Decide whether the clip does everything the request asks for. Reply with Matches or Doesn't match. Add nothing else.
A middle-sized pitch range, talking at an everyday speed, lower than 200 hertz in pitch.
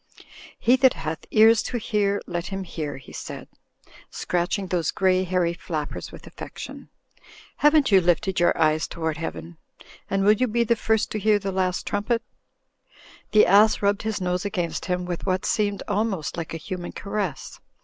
Matches